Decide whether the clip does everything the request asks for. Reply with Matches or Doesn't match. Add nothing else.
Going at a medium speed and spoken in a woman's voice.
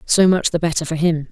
Doesn't match